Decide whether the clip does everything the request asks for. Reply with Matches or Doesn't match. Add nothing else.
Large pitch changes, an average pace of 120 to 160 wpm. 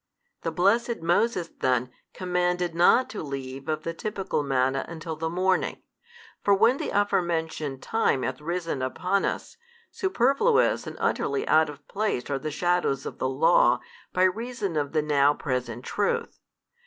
Matches